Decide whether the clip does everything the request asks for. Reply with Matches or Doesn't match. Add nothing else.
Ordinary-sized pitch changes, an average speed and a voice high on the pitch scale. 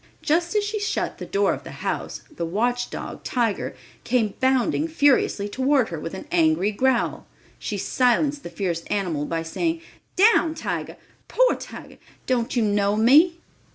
Doesn't match